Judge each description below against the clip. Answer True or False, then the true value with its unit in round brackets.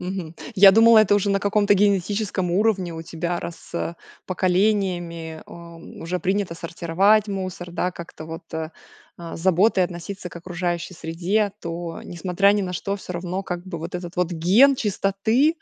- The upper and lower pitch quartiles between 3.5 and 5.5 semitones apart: False (2.7 semitones)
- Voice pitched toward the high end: False (180 Hz)